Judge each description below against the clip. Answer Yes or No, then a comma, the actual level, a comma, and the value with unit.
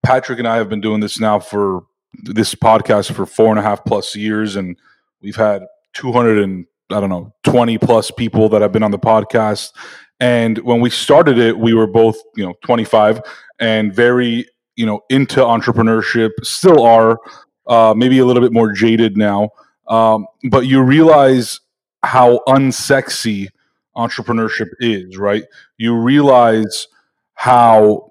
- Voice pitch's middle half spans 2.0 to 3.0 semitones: Yes, narrow, 2.4 semitones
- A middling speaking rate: Yes, average, 160 wpm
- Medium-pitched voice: No, low, 115 Hz